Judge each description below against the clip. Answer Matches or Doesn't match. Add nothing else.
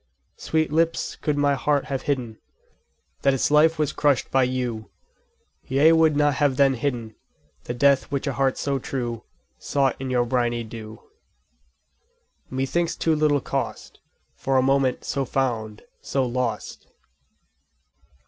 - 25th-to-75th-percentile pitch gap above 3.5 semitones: Doesn't match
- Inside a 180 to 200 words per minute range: Doesn't match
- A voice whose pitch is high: Doesn't match